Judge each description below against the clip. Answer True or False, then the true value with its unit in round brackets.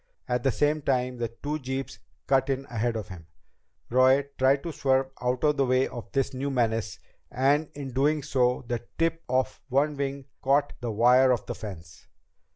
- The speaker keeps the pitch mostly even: True (2.3 semitones)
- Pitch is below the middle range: True (130 Hz)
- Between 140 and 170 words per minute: False (185 wpm)